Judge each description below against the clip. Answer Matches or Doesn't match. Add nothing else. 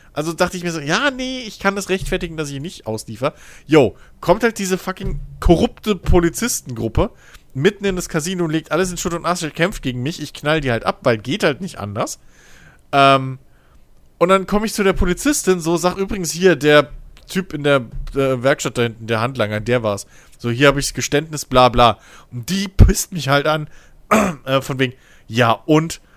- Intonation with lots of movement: Matches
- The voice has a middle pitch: Matches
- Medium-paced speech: Doesn't match